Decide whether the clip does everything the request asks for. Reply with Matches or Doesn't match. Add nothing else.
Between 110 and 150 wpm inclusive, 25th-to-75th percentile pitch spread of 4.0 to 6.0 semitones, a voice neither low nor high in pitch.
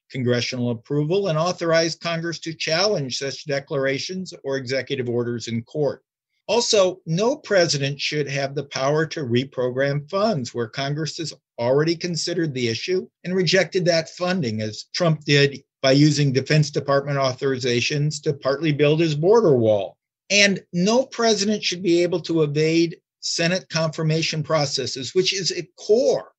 Matches